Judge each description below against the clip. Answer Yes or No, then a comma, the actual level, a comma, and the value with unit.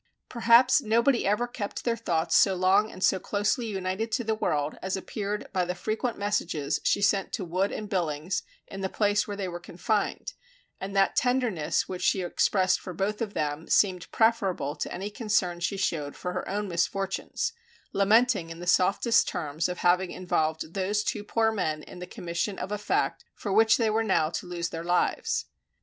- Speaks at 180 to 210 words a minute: Yes, average, 190 wpm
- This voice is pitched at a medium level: No, high, 195 Hz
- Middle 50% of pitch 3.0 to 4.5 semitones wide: Yes, average, 3.4 semitones